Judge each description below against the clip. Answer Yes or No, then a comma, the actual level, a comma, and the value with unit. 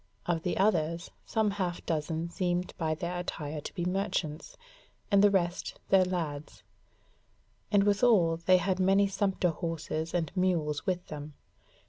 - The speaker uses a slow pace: No, average, 145 wpm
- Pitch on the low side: No, medium, 175 Hz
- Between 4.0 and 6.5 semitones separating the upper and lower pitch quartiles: No, average, 2.9 semitones